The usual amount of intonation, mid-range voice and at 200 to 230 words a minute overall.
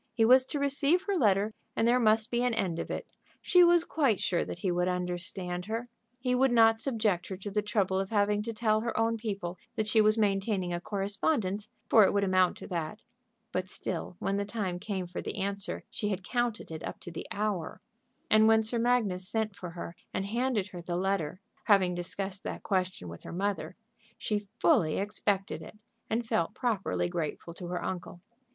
No: average, 3.6 semitones; high, 205 Hz; fast, 205 wpm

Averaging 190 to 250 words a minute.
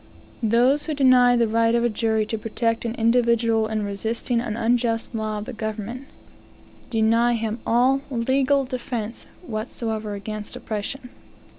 No: average, 140 wpm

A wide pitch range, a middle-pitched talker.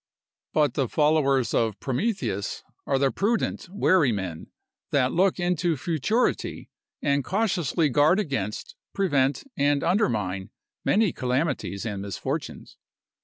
Yes: wide, 6.5 semitones; medium, 145 Hz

